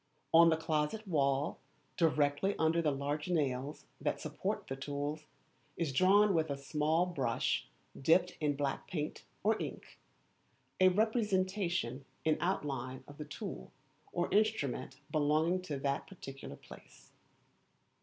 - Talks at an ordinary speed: No, slow, 130 wpm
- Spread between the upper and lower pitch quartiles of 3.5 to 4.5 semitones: Yes, average, 4.2 semitones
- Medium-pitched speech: Yes, medium, 155 Hz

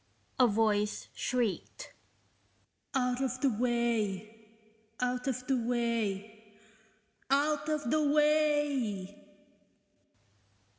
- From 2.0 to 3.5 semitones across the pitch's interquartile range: No, average, 4.3 semitones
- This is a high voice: Yes, high, 245 Hz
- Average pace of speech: No, slow, 85 wpm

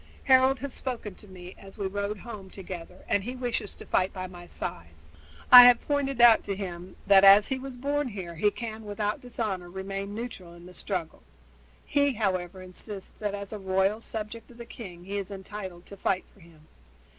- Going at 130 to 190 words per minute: No, average, 200 wpm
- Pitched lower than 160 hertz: No, high, 200 Hz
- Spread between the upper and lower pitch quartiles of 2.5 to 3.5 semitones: No, average, 4.0 semitones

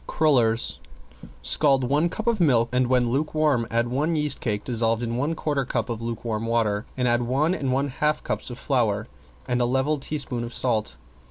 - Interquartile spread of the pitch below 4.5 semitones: Yes, average, 3.8 semitones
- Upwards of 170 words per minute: Yes, average, 190 wpm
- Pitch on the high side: No, low, 125 Hz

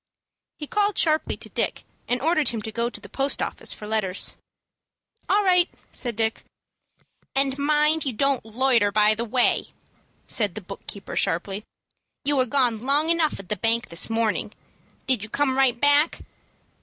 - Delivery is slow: No, average, 170 wpm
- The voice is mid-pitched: No, very high, 250 Hz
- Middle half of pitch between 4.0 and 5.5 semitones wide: Yes, average, 5.0 semitones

